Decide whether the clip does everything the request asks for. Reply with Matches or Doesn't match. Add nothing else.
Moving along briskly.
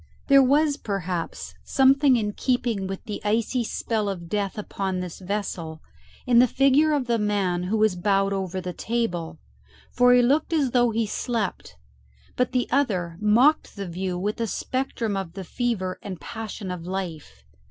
Doesn't match